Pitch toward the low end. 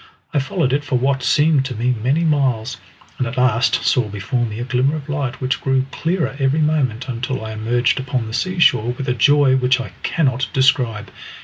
Yes: low, 130 Hz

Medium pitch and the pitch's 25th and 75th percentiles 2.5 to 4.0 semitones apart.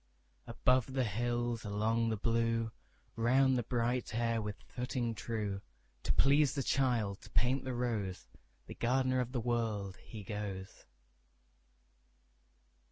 No: low, 115 Hz; average, 3.0 semitones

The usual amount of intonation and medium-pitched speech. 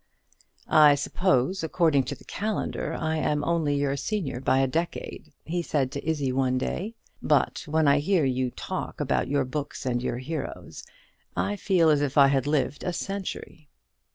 Yes: average, 3.5 semitones; medium, 145 Hz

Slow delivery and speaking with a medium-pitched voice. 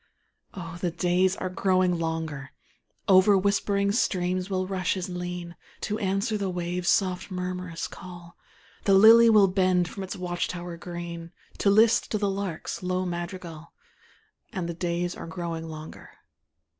No: average, 145 wpm; medium, 180 Hz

